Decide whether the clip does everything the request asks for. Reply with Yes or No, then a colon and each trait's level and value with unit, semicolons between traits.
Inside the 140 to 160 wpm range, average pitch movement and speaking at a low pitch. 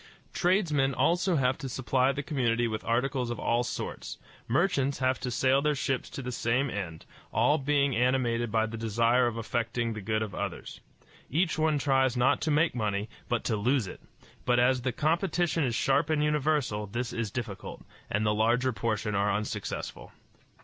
No: average, 180 wpm; average, 3.5 semitones; low, 125 Hz